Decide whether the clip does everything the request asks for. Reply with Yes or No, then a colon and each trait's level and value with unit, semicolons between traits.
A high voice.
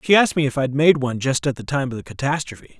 No: low, 135 Hz